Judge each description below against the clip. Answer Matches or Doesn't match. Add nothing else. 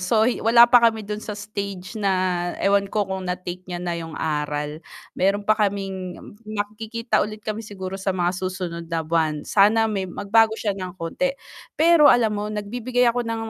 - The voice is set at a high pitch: Matches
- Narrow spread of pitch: Doesn't match